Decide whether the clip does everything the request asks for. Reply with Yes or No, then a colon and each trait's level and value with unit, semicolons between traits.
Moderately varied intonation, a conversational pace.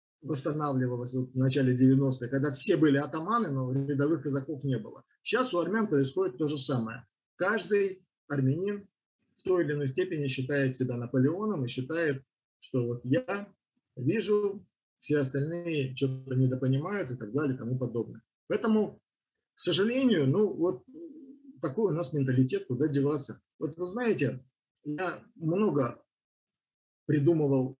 No: wide, 5.7 semitones; average, 135 wpm